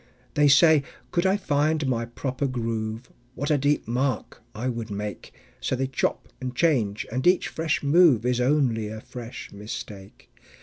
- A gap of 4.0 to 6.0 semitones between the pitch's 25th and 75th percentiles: Yes, average, 4.5 semitones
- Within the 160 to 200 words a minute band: Yes, average, 165 wpm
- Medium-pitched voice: No, low, 130 Hz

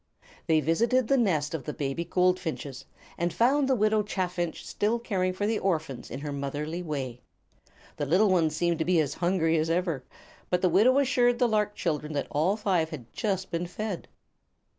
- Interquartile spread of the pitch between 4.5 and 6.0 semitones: Yes, average, 5.0 semitones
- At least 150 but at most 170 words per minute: No, average, 185 wpm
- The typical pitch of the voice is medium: Yes, medium, 175 Hz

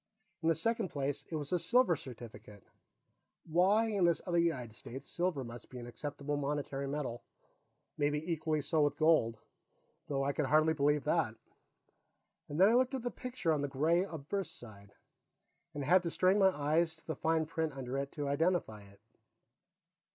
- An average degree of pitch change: Yes, average, 3.8 semitones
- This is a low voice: No, medium, 150 Hz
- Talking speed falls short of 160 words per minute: No, average, 175 wpm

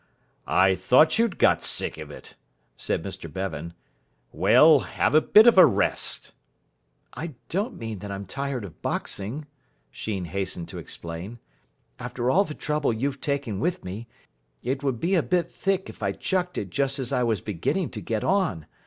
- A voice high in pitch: No, low, 125 Hz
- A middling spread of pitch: No, wide, 8.0 semitones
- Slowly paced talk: No, average, 175 wpm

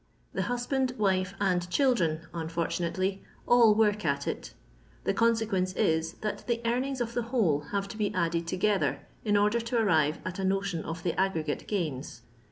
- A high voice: Yes, high, 195 Hz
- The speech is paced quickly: No, average, 170 wpm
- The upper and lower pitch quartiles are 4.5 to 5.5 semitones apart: Yes, average, 5.0 semitones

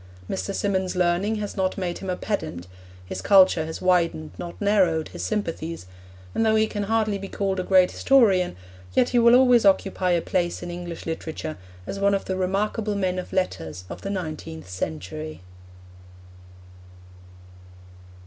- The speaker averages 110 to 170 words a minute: Yes, average, 160 wpm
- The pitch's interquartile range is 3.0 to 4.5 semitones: Yes, average, 3.5 semitones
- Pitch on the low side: No, medium, 185 Hz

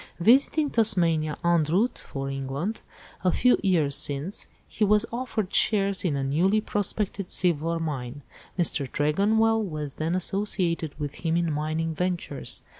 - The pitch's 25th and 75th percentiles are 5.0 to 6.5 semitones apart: Yes, wide, 5.4 semitones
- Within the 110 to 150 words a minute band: Yes, average, 140 wpm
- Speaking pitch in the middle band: Yes, medium, 170 Hz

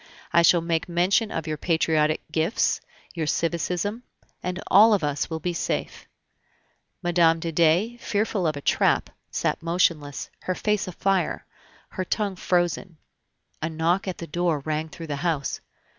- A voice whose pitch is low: No, medium, 170 Hz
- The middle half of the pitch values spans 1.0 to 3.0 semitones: Yes, narrow, 2.4 semitones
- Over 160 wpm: No, average, 155 wpm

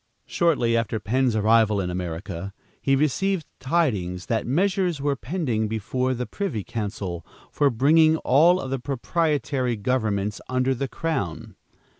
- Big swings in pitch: Yes, wide, 5.8 semitones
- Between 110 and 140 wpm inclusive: Yes, slow, 135 wpm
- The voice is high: No, low, 125 Hz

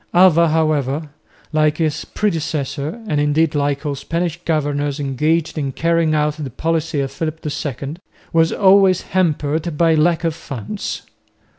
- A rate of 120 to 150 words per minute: Yes, average, 140 wpm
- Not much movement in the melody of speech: Yes, narrow, 2.3 semitones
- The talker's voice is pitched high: No, medium, 155 Hz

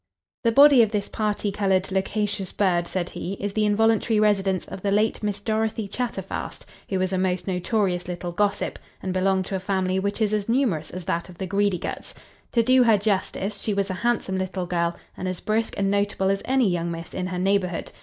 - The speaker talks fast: Yes, fast, 210 wpm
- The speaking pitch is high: Yes, high, 195 Hz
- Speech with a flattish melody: Yes, narrow, 2.3 semitones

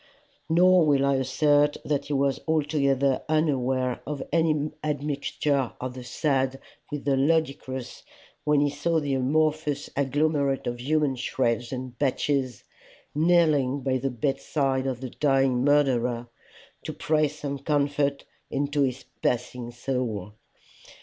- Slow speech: Yes, slow, 130 wpm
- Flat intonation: Yes, narrow, 2.3 semitones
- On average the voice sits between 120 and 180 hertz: Yes, medium, 140 Hz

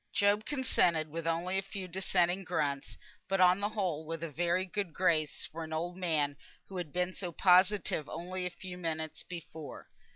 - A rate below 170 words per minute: No, average, 185 wpm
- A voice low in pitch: No, medium, 175 Hz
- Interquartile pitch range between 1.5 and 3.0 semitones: Yes, average, 2.7 semitones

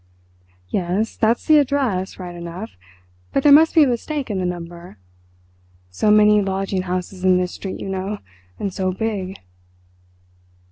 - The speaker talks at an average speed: Yes, average, 150 wpm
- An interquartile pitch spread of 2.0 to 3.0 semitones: No, average, 3.6 semitones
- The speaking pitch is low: No, high, 195 Hz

